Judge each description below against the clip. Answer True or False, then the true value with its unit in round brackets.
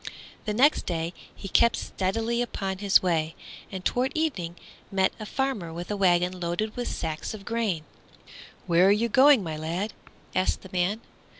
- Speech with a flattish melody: False (4.5 semitones)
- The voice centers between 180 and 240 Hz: True (190 Hz)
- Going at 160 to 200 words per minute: True (170 wpm)